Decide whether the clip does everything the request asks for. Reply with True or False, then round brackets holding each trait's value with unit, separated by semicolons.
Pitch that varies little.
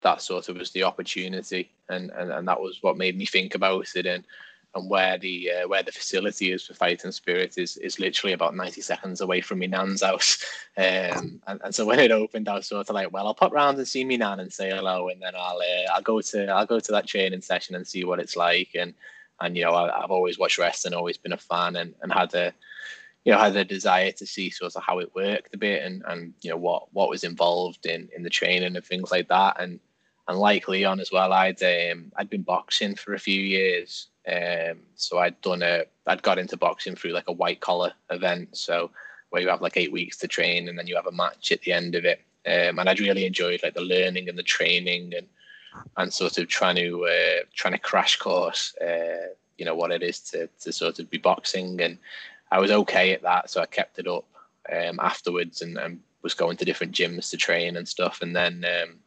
True (1.9 semitones)